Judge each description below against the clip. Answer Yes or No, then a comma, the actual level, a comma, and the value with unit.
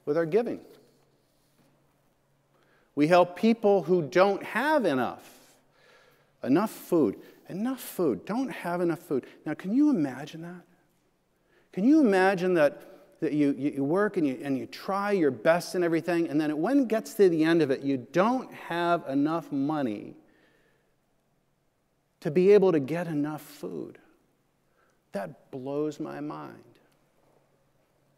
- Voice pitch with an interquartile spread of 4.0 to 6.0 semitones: Yes, average, 5.1 semitones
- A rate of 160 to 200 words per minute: No, average, 140 wpm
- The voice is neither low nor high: Yes, medium, 175 Hz